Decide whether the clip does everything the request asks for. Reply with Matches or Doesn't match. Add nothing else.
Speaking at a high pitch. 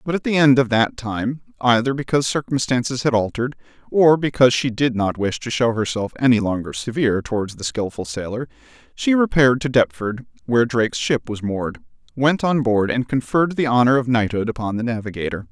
Doesn't match